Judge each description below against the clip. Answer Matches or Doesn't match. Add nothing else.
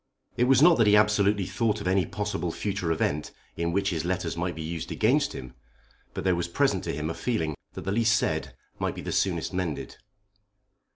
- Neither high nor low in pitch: Doesn't match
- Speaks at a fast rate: Matches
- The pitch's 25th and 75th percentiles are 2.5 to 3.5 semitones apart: Doesn't match